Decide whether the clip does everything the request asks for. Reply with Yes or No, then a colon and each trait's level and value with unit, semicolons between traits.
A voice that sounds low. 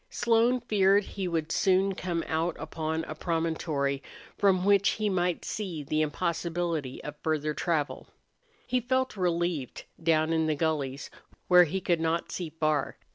No: medium, 170 Hz